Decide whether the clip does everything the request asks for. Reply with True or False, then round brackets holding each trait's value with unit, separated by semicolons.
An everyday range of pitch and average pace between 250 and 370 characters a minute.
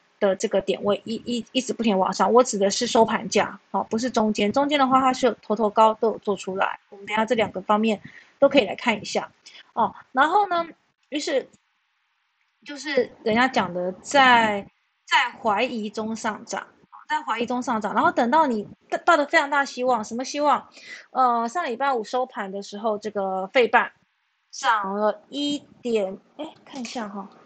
True (4.0 semitones; 270 characters per minute)